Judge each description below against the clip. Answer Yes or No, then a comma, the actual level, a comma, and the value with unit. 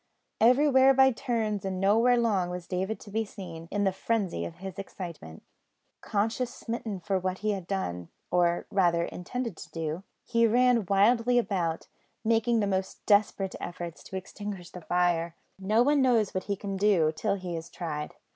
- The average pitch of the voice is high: Yes, high, 195 Hz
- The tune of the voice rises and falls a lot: No, average, 4.3 semitones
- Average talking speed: Yes, average, 175 wpm